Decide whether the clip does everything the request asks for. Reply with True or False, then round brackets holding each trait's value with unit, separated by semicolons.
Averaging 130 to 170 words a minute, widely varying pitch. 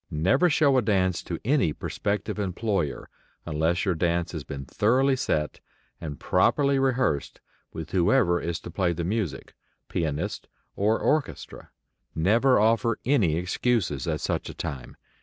True (140 wpm; 6.4 semitones)